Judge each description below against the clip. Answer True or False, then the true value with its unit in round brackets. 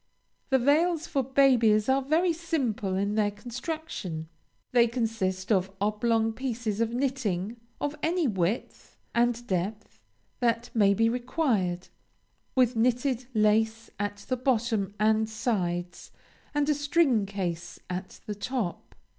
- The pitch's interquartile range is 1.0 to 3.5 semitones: False (4.2 semitones)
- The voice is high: True (225 Hz)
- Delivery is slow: True (130 wpm)